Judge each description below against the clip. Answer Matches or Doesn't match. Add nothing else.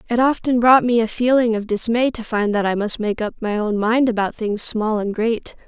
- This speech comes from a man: Doesn't match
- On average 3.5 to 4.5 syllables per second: Doesn't match